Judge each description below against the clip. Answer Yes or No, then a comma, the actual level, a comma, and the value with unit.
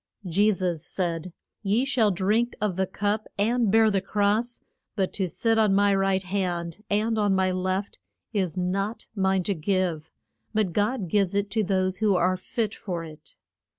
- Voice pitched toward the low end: No, high, 195 Hz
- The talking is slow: No, average, 175 wpm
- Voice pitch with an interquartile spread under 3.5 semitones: Yes, narrow, 2.4 semitones